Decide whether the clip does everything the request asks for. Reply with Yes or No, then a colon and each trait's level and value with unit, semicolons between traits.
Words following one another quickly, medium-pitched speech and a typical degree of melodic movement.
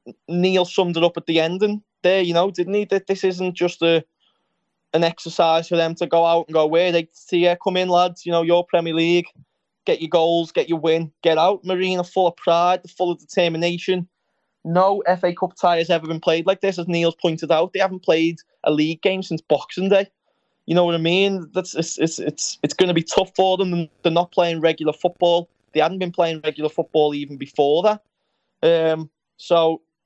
No: fast, 220 wpm; medium, 175 Hz; narrow, 2.0 semitones